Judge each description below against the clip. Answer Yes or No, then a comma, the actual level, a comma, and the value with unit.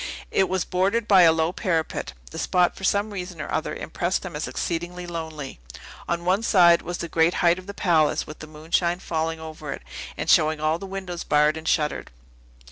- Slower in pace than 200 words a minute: No, fast, 205 wpm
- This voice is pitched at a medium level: Yes, medium, 170 Hz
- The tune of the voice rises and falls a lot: No, narrow, 2.5 semitones